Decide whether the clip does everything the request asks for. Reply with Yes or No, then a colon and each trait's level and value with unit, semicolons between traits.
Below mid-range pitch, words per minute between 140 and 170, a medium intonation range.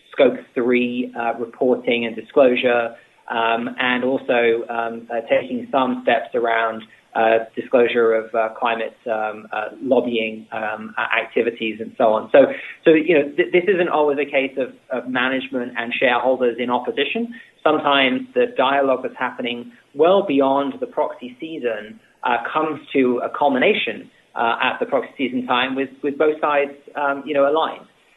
Yes: low, 125 Hz; average, 160 wpm; average, 3.4 semitones